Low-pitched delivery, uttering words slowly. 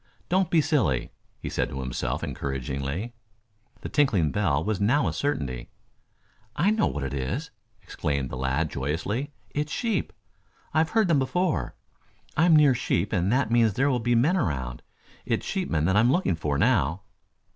No: low, 105 Hz; average, 170 wpm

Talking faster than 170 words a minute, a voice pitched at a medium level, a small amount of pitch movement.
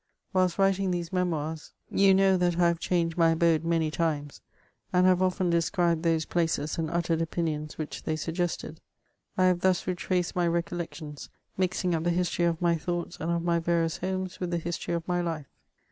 Yes: average, 190 wpm; medium, 170 Hz; narrow, 1.7 semitones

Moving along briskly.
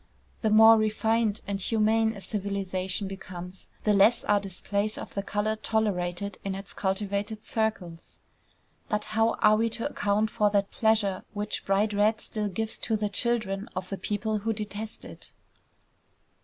No: average, 155 wpm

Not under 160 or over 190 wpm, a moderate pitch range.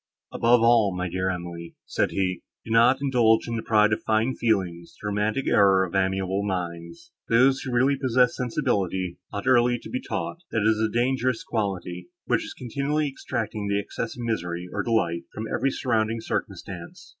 Yes: average, 180 wpm; average, 4.5 semitones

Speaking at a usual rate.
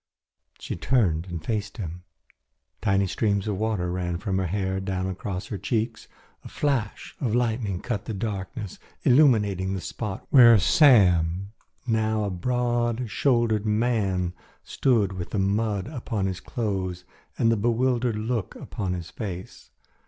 Yes: average, 145 wpm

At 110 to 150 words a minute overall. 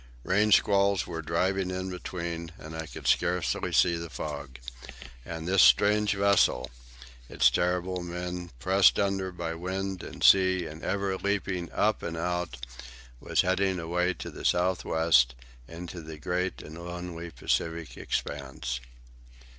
Yes: average, 145 wpm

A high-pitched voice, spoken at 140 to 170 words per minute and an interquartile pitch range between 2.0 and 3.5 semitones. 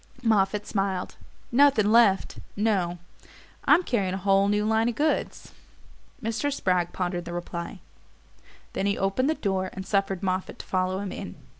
Yes: high, 195 Hz; average, 155 wpm; average, 2.9 semitones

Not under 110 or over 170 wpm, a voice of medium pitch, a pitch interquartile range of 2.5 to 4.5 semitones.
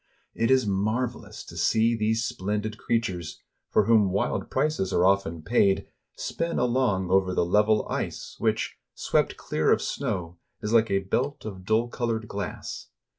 No: average, 155 wpm; low, 105 Hz; average, 3.3 semitones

